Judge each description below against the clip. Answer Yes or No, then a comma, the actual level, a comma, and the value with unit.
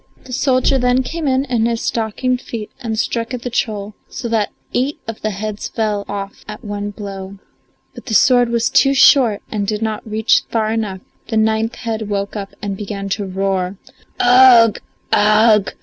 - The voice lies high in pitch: Yes, high, 220 Hz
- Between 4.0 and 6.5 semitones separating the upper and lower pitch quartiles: No, average, 2.9 semitones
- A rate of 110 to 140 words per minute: No, average, 180 wpm